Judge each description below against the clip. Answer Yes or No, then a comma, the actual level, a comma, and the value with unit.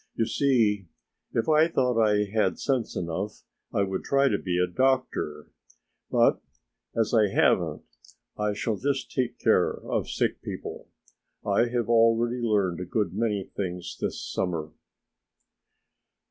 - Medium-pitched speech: No, low, 110 Hz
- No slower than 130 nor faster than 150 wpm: Yes, average, 140 wpm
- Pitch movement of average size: Yes, average, 3.9 semitones